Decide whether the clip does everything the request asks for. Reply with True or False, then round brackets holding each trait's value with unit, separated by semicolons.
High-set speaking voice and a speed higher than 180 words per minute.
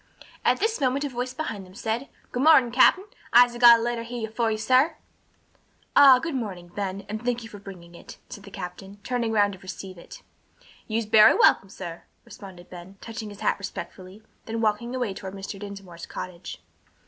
True (215 Hz; 190 wpm)